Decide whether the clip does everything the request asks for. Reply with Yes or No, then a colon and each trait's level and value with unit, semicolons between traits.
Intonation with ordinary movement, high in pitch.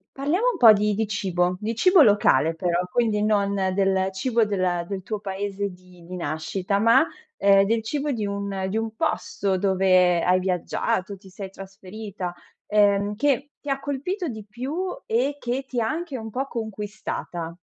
Yes: average, 3.7 semitones; high, 205 Hz